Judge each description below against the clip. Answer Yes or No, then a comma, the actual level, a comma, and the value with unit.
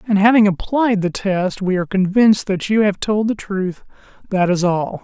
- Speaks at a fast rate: No, average, 190 wpm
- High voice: Yes, high, 200 Hz